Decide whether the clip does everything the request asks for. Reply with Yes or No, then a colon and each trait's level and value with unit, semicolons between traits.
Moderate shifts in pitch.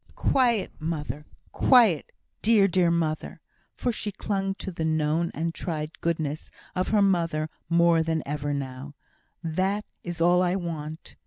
Yes: average, 3.6 semitones